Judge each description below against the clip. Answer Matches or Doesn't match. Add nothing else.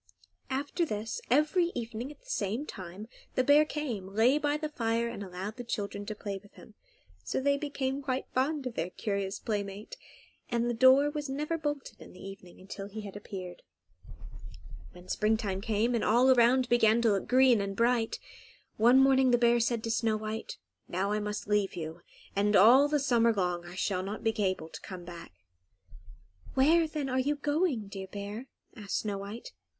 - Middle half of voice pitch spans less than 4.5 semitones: Doesn't match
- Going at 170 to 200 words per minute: Matches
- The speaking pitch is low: Doesn't match